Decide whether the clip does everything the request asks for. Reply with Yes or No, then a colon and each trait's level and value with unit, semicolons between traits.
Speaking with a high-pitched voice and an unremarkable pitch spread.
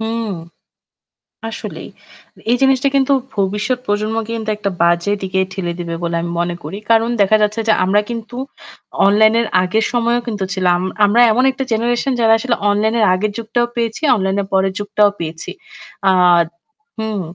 Yes: high, 215 Hz; average, 3.2 semitones